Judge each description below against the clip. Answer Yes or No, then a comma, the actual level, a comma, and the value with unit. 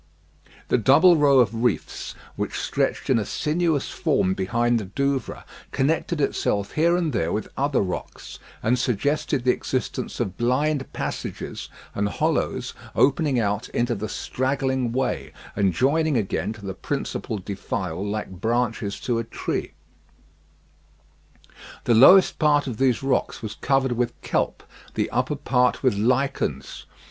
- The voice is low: Yes, low, 125 Hz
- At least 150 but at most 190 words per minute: No, average, 140 wpm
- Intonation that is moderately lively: Yes, average, 4.6 semitones